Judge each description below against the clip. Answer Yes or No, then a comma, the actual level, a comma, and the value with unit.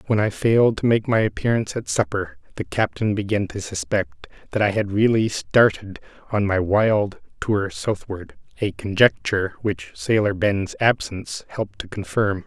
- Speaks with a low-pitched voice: Yes, low, 105 Hz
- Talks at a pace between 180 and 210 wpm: No, average, 155 wpm